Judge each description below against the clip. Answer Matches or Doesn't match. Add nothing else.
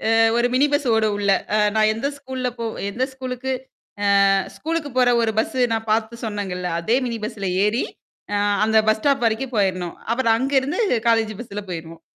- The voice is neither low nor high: Doesn't match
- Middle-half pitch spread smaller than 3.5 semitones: Doesn't match